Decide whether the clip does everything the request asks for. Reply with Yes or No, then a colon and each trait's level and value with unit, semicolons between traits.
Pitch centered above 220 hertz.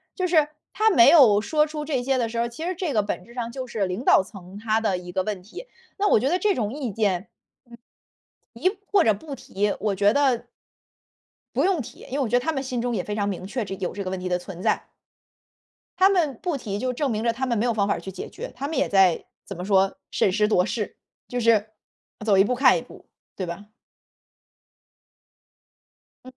Yes: high, 230 Hz